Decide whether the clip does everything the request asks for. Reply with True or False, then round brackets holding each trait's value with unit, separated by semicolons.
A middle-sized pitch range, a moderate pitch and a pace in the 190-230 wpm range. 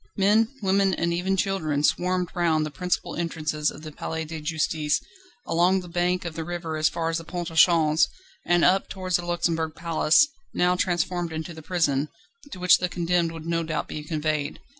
False (2.2 semitones; 170 Hz; 195 wpm)